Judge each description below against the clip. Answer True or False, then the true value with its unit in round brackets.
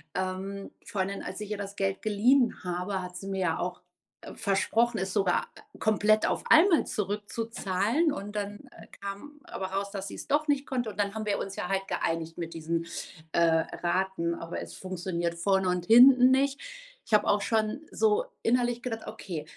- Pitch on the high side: True (200 Hz)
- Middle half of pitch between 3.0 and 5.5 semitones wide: True (3.4 semitones)